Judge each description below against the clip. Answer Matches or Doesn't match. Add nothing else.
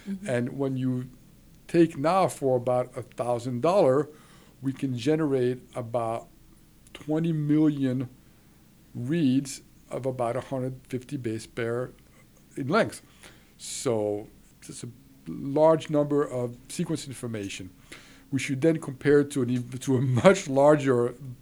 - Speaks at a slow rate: Matches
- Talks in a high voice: Doesn't match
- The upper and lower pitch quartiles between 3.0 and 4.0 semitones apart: Matches